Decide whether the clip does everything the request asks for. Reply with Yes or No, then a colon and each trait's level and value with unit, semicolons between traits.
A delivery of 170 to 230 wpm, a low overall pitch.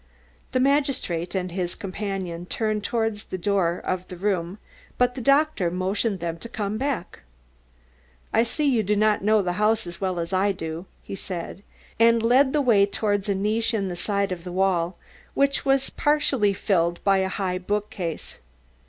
No: average, 180 wpm; high, 200 Hz